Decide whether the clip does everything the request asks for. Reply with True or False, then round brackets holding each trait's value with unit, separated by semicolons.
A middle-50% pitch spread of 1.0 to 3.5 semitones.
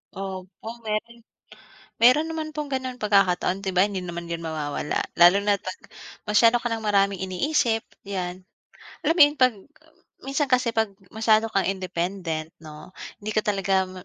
False (3.9 semitones)